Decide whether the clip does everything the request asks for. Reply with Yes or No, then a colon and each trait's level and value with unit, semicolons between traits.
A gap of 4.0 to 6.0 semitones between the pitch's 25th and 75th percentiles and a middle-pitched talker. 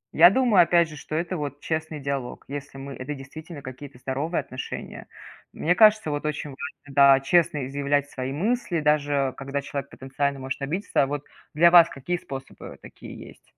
No: average, 3.3 semitones; medium, 145 Hz